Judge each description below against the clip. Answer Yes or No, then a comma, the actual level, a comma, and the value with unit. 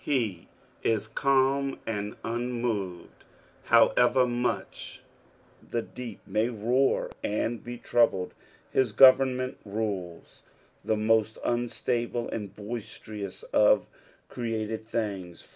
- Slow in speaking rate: Yes, slow, 95 wpm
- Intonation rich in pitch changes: No, narrow, 2.6 semitones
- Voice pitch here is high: No, low, 115 Hz